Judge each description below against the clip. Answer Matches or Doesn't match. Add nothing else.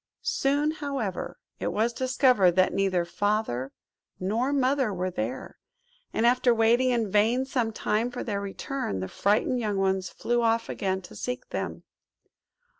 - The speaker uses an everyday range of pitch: Matches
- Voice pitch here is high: Matches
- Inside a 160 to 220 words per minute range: Doesn't match